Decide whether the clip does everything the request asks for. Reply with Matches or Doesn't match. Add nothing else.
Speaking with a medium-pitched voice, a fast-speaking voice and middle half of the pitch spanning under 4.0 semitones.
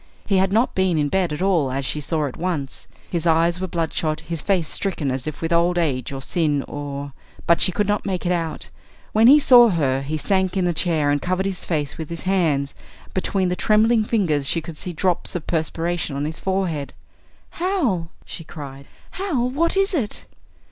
Doesn't match